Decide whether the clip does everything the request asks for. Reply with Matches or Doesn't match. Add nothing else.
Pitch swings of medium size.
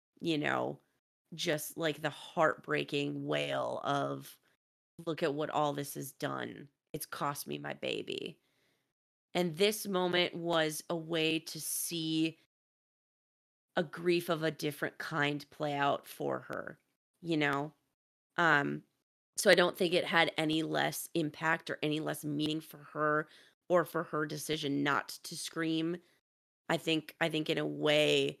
Doesn't match